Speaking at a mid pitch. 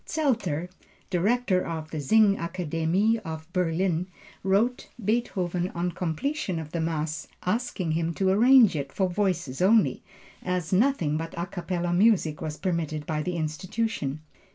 Yes: medium, 180 Hz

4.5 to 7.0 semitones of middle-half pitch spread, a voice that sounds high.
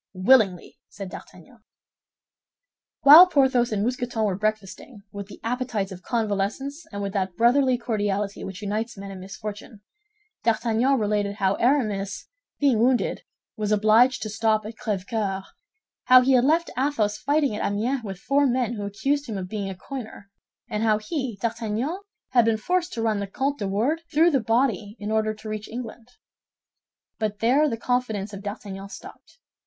No: average, 3.8 semitones; high, 220 Hz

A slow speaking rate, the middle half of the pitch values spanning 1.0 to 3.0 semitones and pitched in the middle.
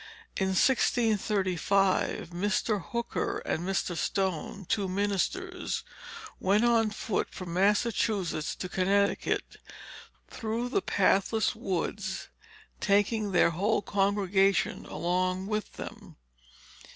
No: slow, 95 wpm; narrow, 2.5 semitones; high, 200 Hz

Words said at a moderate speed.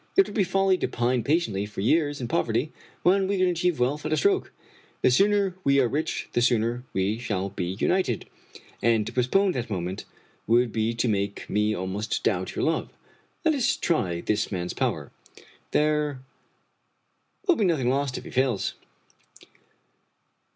Yes: average, 170 wpm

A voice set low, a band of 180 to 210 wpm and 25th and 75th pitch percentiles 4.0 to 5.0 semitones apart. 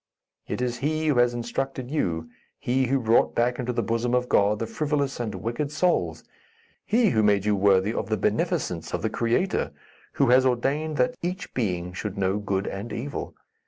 Yes: low, 120 Hz; average, 190 wpm; average, 4.7 semitones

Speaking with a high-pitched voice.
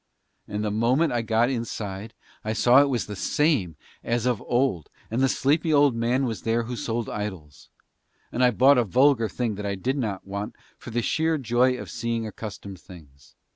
No: low, 115 Hz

